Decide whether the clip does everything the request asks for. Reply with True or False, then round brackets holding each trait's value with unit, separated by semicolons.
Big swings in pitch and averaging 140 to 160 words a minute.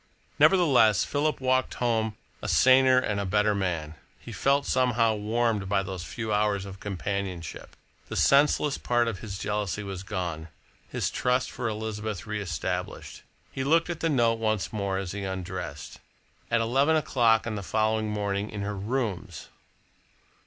False (3.8 semitones; 155 wpm)